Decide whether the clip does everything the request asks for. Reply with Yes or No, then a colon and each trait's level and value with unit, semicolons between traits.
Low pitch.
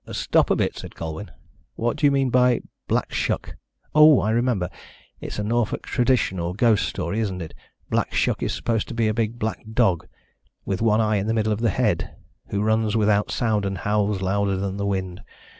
Yes: low, 105 Hz